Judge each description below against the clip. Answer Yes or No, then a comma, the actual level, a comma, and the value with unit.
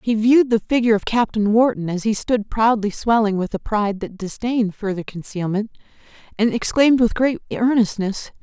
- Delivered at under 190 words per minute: Yes, average, 170 wpm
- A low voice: No, high, 215 Hz